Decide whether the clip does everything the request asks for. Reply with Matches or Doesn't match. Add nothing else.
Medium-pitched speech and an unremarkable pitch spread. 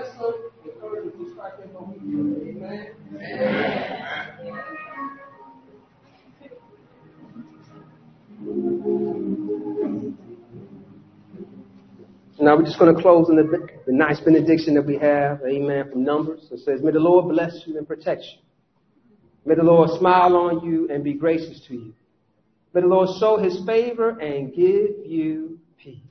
Doesn't match